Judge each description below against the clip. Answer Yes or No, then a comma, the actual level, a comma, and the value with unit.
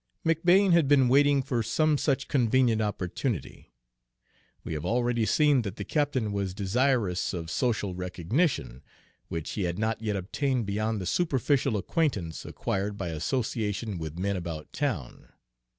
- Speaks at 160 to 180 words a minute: No, average, 145 wpm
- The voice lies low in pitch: Yes, low, 110 Hz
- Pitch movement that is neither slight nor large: No, wide, 6.4 semitones